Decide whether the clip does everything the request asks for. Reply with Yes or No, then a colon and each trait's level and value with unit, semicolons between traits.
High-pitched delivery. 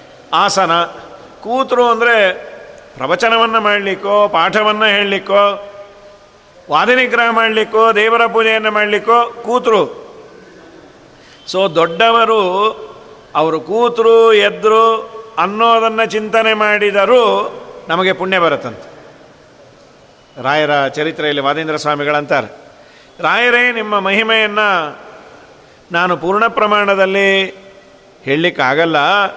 Yes: high, 210 Hz